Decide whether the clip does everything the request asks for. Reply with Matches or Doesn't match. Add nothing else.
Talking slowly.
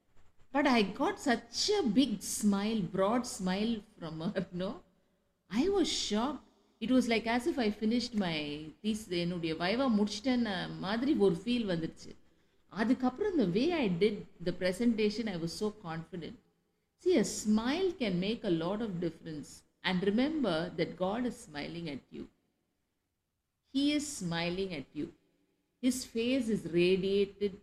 Matches